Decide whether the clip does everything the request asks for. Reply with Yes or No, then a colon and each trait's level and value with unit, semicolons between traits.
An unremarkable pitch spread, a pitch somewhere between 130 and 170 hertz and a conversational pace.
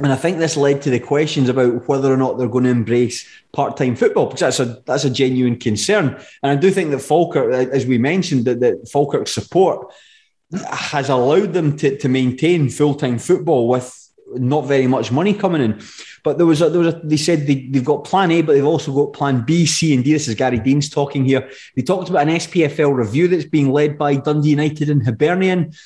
No: average, 3.6 semitones; medium, 140 Hz; fast, 225 wpm